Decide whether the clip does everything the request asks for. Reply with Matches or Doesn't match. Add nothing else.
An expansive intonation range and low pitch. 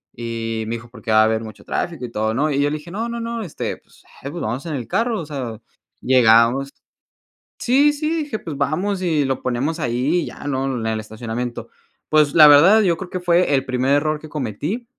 Doesn't match